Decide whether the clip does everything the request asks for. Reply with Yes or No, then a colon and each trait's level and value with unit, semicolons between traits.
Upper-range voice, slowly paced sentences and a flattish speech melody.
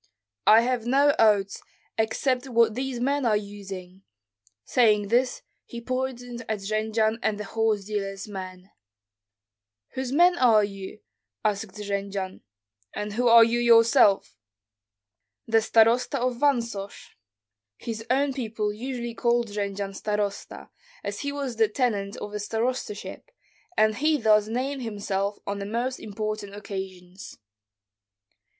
No: high, 220 Hz; slow, 130 wpm; average, 3.2 semitones